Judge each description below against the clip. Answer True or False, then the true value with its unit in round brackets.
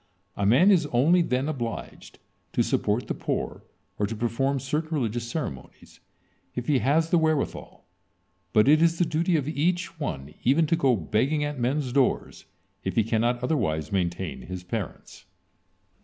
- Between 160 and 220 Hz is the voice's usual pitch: False (135 Hz)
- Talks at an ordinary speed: True (160 wpm)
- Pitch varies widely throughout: True (5.8 semitones)